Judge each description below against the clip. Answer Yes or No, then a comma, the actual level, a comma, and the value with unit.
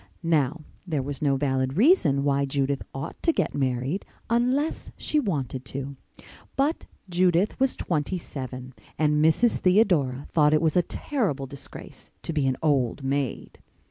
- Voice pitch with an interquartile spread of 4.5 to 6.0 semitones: Yes, average, 5.3 semitones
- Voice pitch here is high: No, medium, 150 Hz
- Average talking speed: Yes, average, 150 wpm